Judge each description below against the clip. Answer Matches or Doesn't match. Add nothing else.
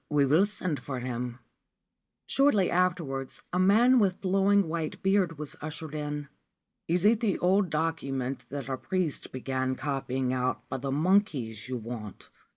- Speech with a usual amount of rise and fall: Doesn't match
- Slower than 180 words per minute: Matches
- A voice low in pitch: Doesn't match